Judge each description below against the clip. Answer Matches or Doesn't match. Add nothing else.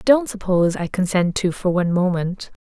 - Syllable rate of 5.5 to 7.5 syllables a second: Doesn't match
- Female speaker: Matches